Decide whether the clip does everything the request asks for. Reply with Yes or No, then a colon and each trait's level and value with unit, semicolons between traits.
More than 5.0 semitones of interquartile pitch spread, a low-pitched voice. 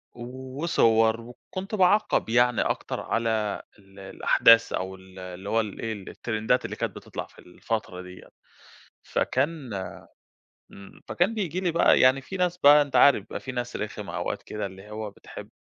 Yes: wide, 5.6 semitones; low, 115 Hz